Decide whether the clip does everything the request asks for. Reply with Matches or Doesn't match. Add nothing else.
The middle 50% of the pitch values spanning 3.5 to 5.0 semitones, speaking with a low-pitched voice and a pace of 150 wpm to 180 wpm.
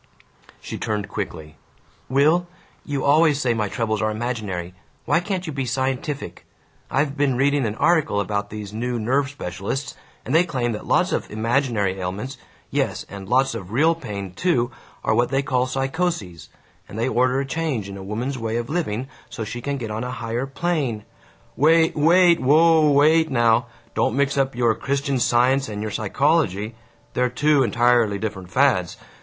Matches